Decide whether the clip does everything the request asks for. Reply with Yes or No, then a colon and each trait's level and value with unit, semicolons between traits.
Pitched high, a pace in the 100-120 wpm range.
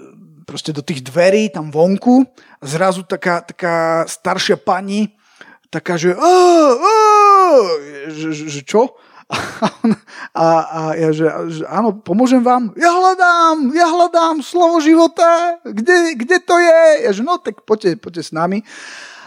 No: high, 220 Hz; average, 140 wpm